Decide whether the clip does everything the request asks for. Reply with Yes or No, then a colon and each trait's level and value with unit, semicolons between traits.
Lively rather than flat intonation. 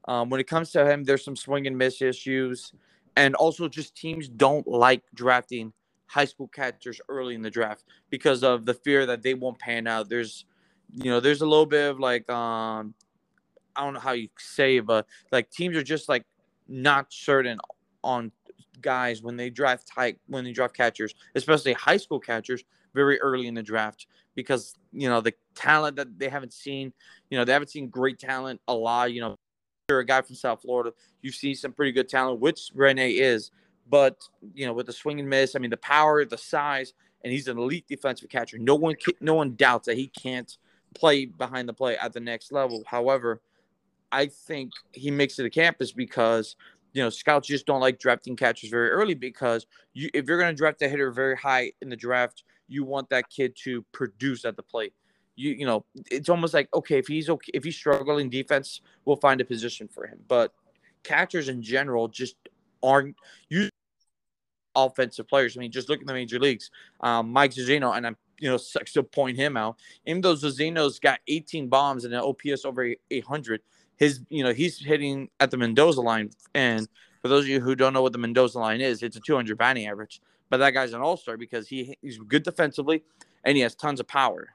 No: average, 2.7 semitones